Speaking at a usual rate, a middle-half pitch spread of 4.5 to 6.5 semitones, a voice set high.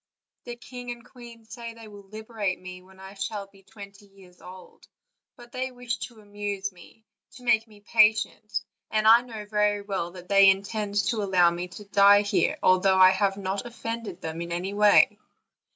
No: average, 190 wpm; narrow, 2.6 semitones; high, 205 Hz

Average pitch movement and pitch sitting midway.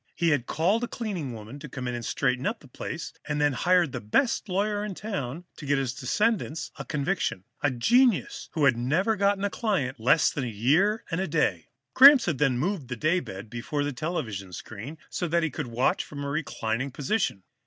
No: wide, 7.1 semitones; medium, 150 Hz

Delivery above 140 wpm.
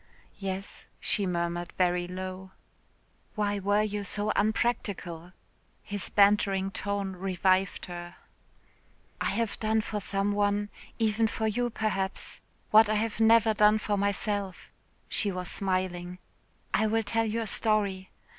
No: slow, 135 wpm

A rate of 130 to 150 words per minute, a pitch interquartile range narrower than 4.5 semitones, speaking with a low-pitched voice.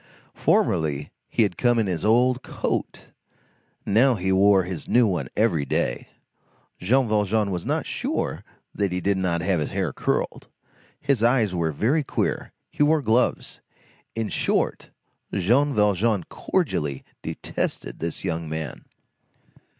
No: average, 140 wpm; average, 5.1 semitones; low, 100 Hz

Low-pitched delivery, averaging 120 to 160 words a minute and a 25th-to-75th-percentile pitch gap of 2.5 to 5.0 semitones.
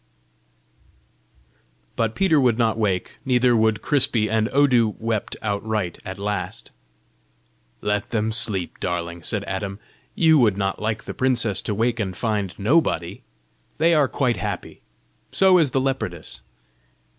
Yes: low, 110 Hz; slow, 135 wpm; average, 3.9 semitones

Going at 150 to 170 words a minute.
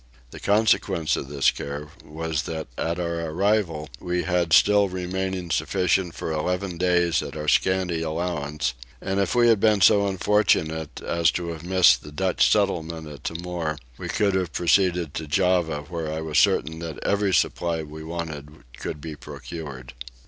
Yes: average, 165 wpm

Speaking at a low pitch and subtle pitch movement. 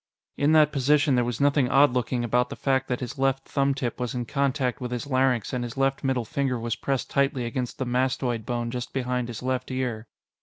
Yes: low, 130 Hz; narrow, 1.9 semitones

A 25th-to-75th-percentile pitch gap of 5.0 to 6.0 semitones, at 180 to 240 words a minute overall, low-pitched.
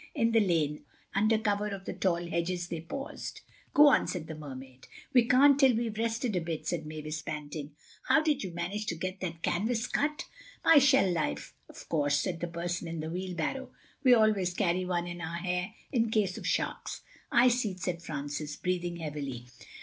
No: wide, 5.4 semitones; average, 190 wpm; medium, 180 Hz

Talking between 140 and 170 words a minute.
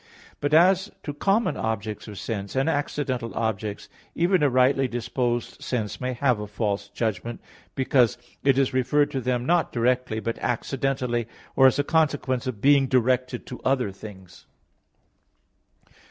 Yes: average, 150 wpm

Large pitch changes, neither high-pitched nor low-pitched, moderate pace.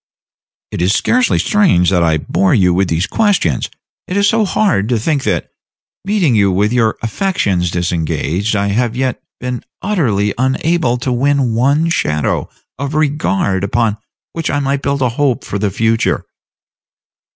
No: wide, 6.8 semitones; low, 120 Hz; average, 160 wpm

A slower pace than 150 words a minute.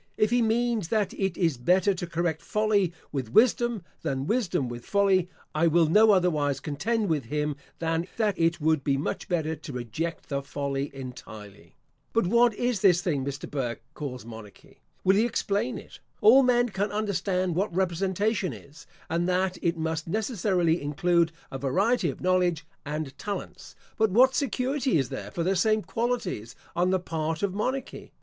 No: average, 175 wpm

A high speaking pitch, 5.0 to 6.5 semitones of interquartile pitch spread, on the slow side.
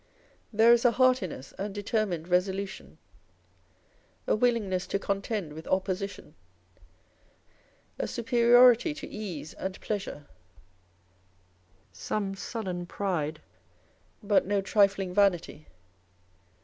No: high, 200 Hz; average, 3.3 semitones; slow, 95 wpm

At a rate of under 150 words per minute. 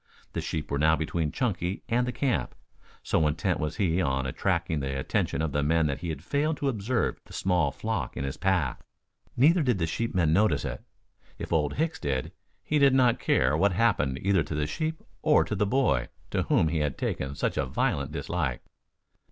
No: average, 200 wpm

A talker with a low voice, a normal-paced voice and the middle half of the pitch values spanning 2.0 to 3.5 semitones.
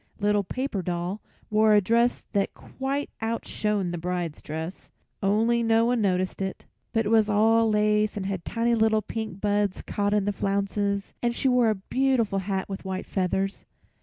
No: high, 210 Hz; average, 175 wpm; narrow, 2.6 semitones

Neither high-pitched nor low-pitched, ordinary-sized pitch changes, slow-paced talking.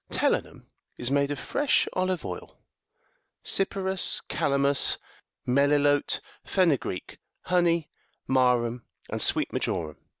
No: medium, 145 Hz; wide, 5.7 semitones; slow, 100 wpm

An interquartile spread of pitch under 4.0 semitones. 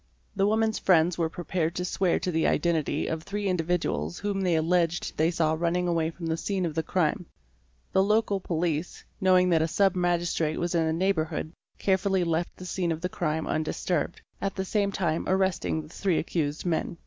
Yes: average, 2.7 semitones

